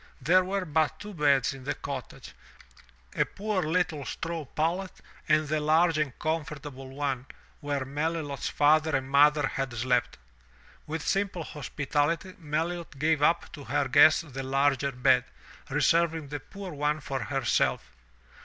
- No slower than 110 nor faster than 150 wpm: Yes, average, 145 wpm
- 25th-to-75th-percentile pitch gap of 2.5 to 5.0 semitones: Yes, average, 3.0 semitones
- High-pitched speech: No, medium, 150 Hz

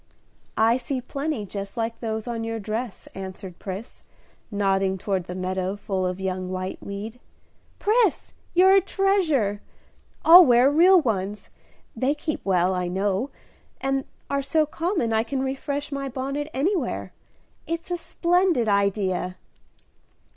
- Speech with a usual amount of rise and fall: No, wide, 7.0 semitones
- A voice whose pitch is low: No, high, 230 Hz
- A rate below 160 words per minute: Yes, slow, 135 wpm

